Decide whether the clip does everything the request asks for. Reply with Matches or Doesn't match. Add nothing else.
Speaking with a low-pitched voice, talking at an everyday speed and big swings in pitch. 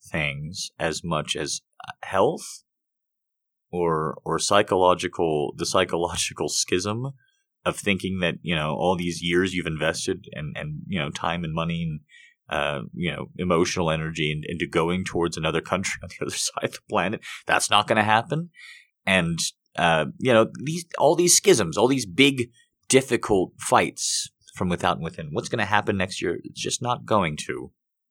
Matches